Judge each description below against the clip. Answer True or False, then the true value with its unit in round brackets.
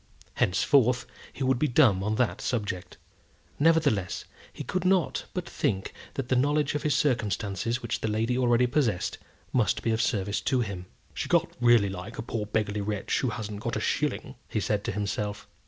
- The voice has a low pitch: True (115 Hz)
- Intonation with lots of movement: False (3.9 semitones)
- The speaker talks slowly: False (185 wpm)